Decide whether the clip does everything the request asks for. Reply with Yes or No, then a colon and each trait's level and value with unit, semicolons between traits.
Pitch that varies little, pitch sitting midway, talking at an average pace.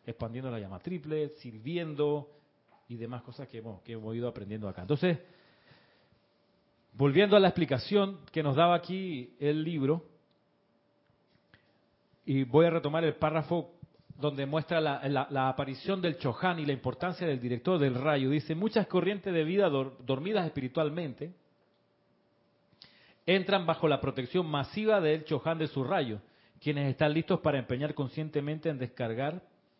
No: average, 4.3 semitones; medium, 150 Hz; average, 145 wpm